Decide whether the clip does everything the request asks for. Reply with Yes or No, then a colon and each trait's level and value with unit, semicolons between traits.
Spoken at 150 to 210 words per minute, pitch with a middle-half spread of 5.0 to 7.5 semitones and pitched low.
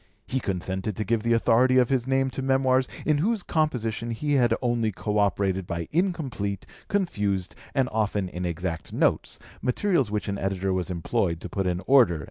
Yes: average, 175 wpm; wide, 5.6 semitones; low, 110 Hz